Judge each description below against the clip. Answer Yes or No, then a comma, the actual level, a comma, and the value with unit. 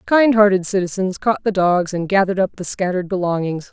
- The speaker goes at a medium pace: Yes, average, 195 wpm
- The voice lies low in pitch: No, high, 190 Hz